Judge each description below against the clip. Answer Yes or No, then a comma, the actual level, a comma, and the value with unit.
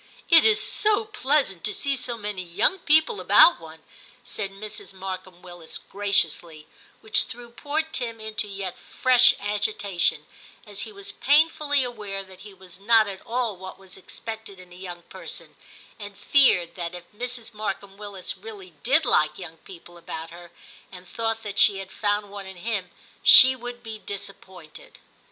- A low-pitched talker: No, high, 205 Hz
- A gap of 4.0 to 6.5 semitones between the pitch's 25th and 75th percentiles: Yes, average, 4.3 semitones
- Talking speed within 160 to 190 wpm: Yes, average, 170 wpm